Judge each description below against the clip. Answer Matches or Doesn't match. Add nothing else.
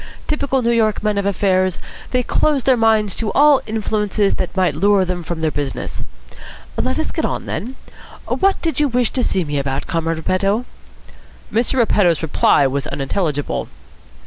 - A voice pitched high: Matches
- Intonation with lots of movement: Matches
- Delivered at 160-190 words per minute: Matches